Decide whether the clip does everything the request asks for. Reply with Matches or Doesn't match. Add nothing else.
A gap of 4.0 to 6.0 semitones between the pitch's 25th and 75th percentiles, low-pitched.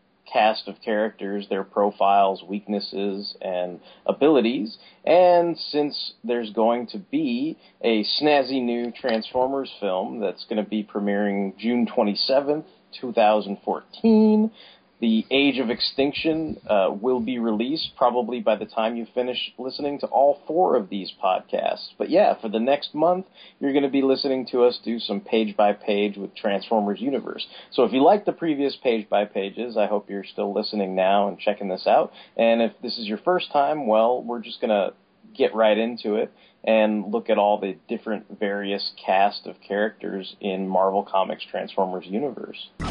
Matches